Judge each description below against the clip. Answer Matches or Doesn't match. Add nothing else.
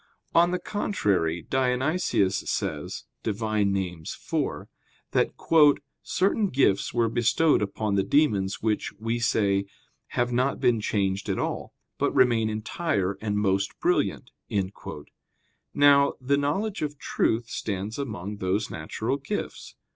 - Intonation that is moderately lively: Doesn't match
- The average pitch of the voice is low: Matches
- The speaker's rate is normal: Doesn't match